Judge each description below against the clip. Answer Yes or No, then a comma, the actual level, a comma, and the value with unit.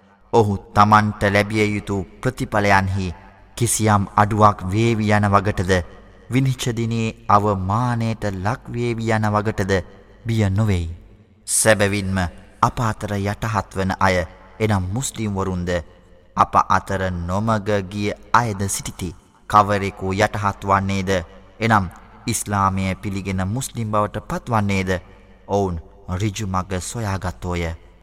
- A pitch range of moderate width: No, narrow, 2.2 semitones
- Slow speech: No, average, 80 wpm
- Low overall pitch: Yes, low, 100 Hz